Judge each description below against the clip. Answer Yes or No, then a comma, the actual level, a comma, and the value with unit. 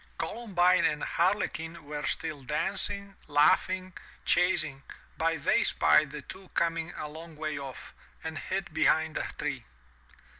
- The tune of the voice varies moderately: Yes, average, 3.5 semitones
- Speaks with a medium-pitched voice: Yes, medium, 165 Hz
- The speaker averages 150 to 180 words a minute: No, average, 140 wpm